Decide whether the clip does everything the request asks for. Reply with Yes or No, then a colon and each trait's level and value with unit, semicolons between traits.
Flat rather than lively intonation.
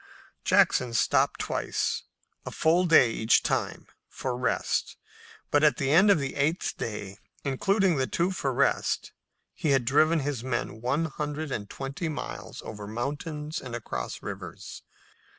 No: average, 4.5 semitones